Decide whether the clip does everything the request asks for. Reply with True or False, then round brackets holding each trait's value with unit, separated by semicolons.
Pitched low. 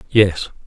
True (95 Hz)